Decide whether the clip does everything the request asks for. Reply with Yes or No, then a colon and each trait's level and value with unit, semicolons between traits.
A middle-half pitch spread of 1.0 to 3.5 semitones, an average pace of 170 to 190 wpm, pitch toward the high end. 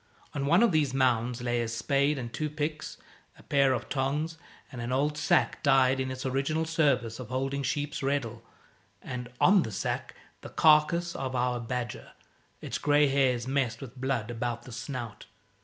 No: average, 3.1 semitones; average, 175 wpm; low, 135 Hz